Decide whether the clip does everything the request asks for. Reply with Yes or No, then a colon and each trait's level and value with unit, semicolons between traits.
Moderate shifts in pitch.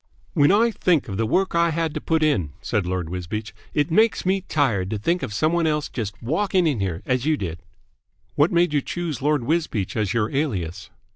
No: wide, 8.3 semitones